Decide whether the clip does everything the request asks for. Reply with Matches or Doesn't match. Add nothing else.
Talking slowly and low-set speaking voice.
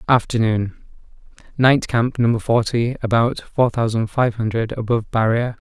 Matches